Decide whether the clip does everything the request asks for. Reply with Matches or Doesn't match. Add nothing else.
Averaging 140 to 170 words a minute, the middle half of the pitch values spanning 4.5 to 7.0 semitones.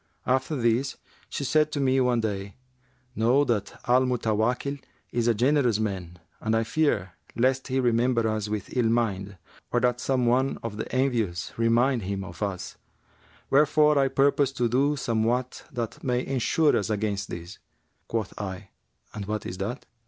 Doesn't match